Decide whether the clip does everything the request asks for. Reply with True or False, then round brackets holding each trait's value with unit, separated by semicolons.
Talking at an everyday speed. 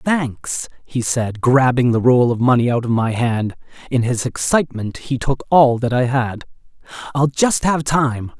True (165 wpm)